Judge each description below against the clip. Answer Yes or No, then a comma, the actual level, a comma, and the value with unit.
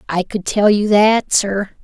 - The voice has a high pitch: Yes, high, 205 Hz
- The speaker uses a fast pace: No, average, 195 wpm